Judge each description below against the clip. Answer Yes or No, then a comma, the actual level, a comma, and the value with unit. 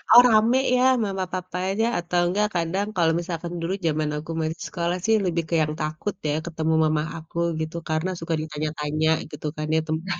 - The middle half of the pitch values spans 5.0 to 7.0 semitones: No, average, 2.8 semitones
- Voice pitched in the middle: Yes, medium, 165 Hz